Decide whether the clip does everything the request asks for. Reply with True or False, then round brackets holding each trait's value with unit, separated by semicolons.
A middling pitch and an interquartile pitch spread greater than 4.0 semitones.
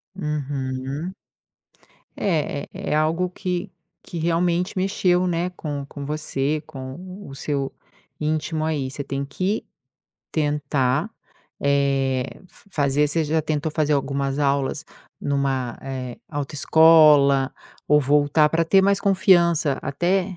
False (150 Hz; 3.4 semitones)